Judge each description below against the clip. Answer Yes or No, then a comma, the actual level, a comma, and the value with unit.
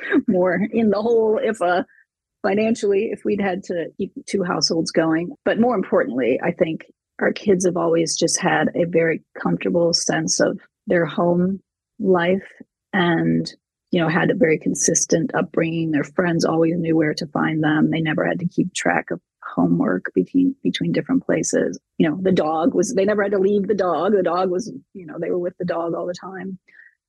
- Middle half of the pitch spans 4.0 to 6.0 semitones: No, average, 3.3 semitones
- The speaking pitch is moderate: Yes, medium, 180 Hz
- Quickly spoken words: No, average, 195 wpm